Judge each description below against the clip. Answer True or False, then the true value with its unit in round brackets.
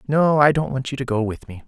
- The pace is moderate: False (320 wpm)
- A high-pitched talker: False (130 Hz)